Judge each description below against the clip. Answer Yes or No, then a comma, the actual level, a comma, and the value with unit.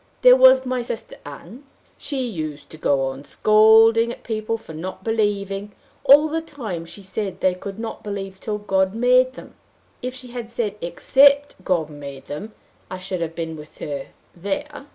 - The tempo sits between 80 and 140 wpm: No, average, 175 wpm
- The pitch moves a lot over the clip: Yes, wide, 5.9 semitones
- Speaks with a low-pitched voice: No, high, 205 Hz